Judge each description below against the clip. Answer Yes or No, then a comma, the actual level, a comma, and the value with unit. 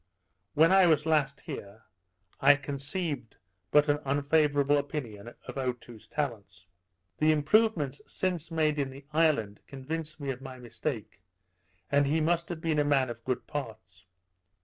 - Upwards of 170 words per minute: No, average, 150 wpm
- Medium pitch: Yes, medium, 145 Hz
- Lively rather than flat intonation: No, average, 3.4 semitones